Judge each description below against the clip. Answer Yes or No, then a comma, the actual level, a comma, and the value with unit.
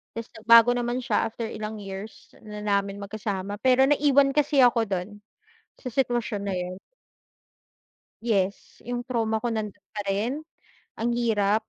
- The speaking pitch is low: No, high, 220 Hz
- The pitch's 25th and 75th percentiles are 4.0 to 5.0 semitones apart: No, average, 3.2 semitones